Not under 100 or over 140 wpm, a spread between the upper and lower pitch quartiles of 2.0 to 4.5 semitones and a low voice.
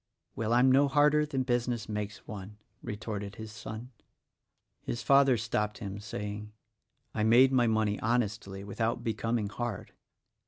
Yes: slow, 135 wpm; average, 2.7 semitones; low, 110 Hz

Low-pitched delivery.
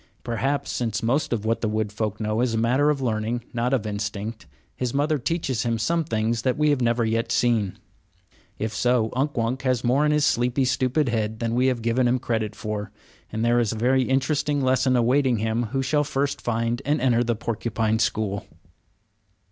Yes: low, 120 Hz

